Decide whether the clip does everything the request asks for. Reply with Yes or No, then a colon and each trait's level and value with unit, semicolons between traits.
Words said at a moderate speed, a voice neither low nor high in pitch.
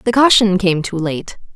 No: average, 195 wpm; high, 195 Hz